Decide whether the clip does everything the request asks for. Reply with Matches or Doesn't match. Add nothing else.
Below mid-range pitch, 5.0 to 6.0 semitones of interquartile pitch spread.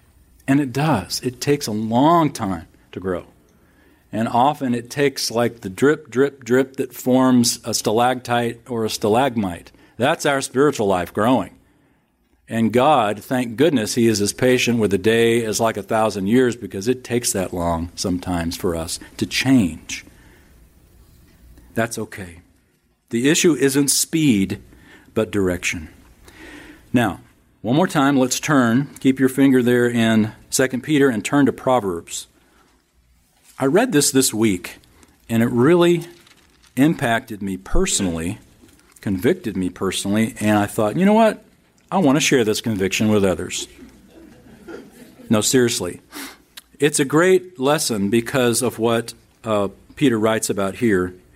Matches